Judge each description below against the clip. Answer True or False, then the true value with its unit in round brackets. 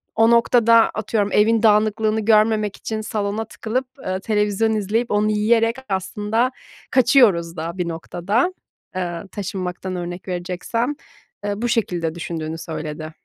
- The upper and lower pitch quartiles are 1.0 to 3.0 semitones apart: False (3.9 semitones)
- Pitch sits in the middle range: False (210 Hz)